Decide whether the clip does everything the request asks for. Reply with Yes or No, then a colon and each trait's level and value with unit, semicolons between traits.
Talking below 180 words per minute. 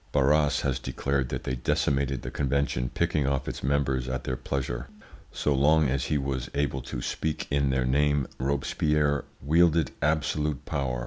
Yes: average, 165 wpm